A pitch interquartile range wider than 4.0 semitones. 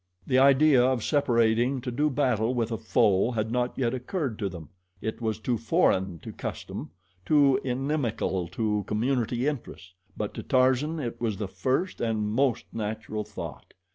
No: average, 3.6 semitones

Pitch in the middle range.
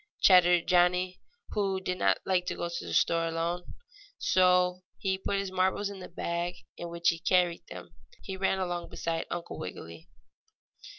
Yes: medium, 180 Hz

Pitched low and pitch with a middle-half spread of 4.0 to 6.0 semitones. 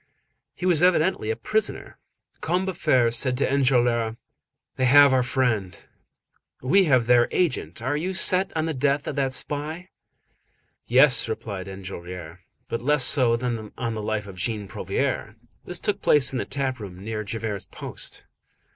Yes: low, 125 Hz; average, 4.8 semitones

